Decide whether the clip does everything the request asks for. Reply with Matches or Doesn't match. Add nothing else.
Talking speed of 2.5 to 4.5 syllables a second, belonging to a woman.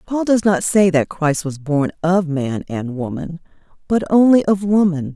Matches